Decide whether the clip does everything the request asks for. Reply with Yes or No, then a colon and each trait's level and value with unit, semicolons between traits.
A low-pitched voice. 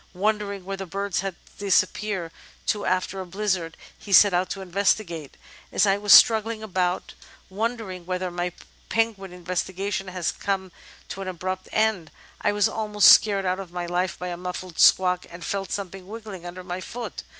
No: high, 190 Hz